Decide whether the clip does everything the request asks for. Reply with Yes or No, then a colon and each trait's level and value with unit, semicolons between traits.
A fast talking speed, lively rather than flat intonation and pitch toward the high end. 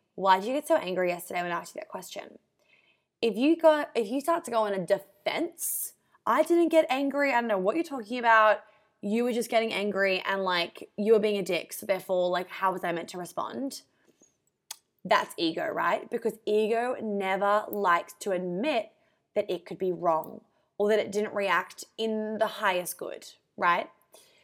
No: average, 195 wpm; wide, 5.8 semitones; high, 215 Hz